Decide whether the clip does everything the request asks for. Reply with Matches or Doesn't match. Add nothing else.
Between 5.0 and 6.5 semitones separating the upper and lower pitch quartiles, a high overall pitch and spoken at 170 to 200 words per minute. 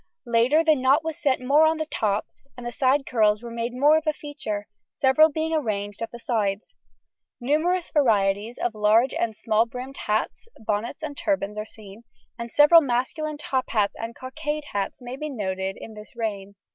Matches